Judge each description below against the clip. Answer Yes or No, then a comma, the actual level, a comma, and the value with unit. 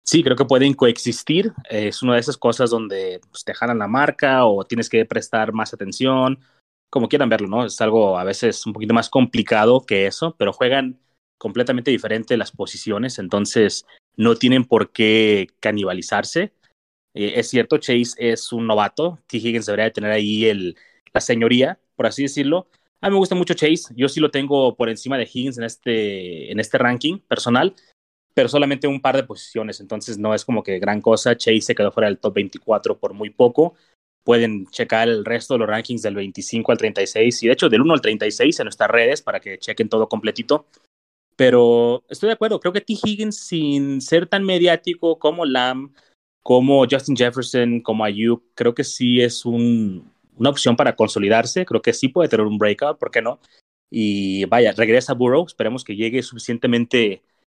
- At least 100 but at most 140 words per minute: No, fast, 190 wpm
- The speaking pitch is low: Yes, low, 120 Hz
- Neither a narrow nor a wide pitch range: Yes, average, 4.1 semitones